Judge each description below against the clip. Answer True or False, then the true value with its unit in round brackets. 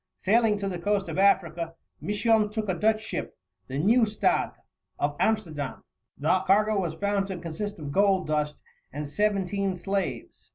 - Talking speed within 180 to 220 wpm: False (155 wpm)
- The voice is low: False (195 Hz)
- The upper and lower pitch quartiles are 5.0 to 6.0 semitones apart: False (3.8 semitones)